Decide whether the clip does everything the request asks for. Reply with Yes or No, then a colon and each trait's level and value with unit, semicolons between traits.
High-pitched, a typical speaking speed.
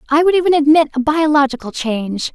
Yes: very high, 290 Hz; average, 180 wpm